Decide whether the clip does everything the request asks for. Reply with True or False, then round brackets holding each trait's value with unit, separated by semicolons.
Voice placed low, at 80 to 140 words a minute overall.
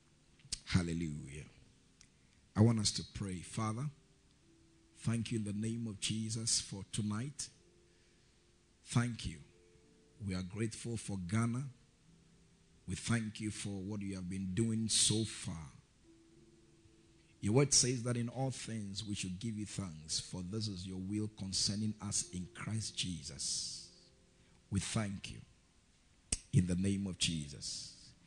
True (105 Hz; 135 wpm)